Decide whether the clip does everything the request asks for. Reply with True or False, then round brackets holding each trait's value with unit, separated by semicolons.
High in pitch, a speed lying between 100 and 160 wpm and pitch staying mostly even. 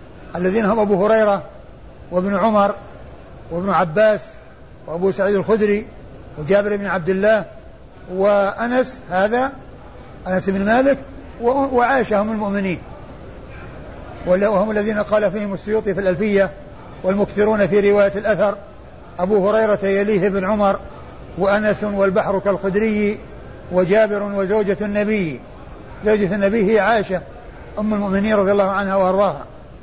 True (200 Hz; 110 wpm; 1.8 semitones)